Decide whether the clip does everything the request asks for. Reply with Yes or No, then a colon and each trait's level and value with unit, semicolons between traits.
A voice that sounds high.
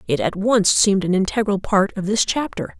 Yes: high, 200 Hz